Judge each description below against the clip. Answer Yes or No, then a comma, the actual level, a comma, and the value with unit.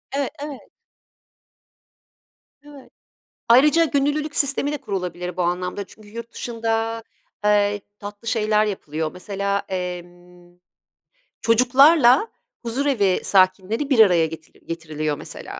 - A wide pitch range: Yes, wide, 6.3 semitones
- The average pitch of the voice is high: Yes, high, 210 Hz